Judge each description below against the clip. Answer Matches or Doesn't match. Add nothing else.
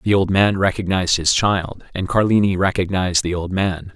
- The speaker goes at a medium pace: Matches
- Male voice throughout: Matches